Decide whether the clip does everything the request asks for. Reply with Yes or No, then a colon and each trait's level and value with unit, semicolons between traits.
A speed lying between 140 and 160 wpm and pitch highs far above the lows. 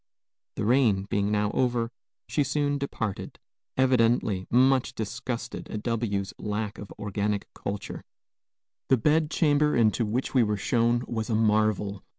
No: average, 145 wpm; average, 3.5 semitones